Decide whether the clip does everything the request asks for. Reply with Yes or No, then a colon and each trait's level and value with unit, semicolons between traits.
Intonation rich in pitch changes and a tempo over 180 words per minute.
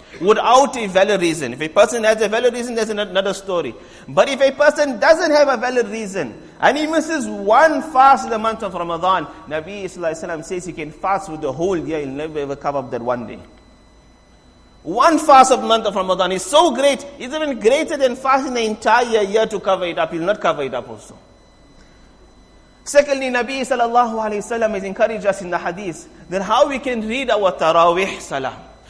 Yes: wide, 6.6 semitones; average, 200 wpm